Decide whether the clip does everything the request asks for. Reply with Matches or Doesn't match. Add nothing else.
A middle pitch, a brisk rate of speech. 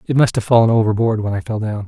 Doesn't match